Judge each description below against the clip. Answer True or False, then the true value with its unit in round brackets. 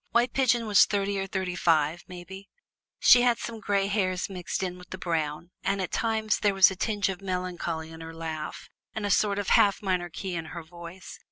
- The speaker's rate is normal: False (210 wpm)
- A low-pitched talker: False (190 Hz)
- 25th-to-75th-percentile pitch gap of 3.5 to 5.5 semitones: False (2.8 semitones)